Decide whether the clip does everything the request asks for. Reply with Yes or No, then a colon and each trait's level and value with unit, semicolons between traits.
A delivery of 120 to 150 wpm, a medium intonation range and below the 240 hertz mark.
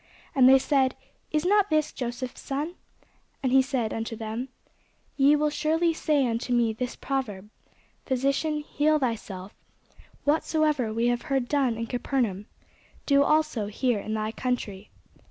No: average, 145 wpm; average, 4.4 semitones; very high, 260 Hz